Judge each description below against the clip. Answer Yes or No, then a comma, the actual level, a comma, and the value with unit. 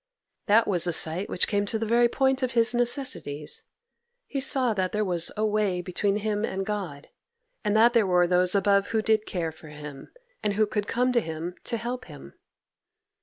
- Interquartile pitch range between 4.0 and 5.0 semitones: Yes, average, 4.4 semitones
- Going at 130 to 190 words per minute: No, average, 200 wpm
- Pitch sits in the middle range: No, high, 205 Hz